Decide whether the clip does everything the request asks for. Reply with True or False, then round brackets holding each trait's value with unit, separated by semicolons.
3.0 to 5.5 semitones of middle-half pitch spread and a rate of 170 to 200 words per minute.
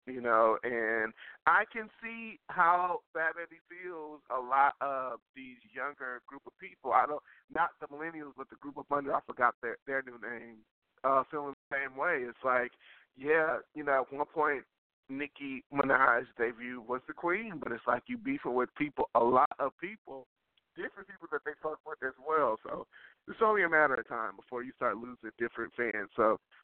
True (5.0 semitones; 190 wpm)